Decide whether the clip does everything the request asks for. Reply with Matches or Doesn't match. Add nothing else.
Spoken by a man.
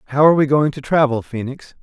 Matches